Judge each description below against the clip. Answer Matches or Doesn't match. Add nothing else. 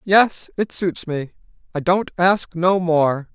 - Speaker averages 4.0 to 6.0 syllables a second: Doesn't match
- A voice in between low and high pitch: Matches